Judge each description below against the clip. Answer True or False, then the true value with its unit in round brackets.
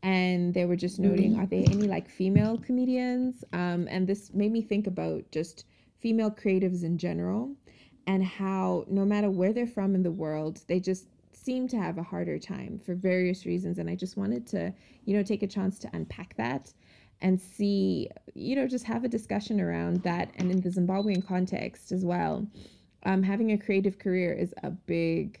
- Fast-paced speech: False (195 wpm)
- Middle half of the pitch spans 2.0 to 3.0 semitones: True (2.4 semitones)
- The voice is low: False (195 Hz)